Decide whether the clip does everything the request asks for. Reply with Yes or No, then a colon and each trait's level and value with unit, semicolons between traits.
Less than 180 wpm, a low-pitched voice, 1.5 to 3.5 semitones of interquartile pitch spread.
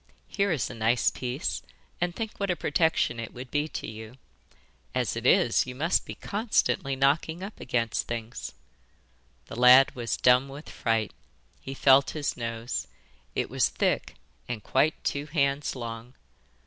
No: average, 160 wpm; low, 130 Hz; average, 4.5 semitones